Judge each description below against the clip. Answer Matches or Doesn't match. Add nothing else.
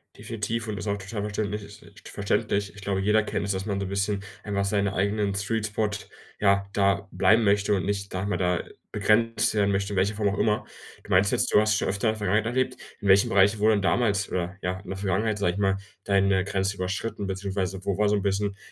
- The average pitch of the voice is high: Doesn't match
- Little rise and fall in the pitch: Matches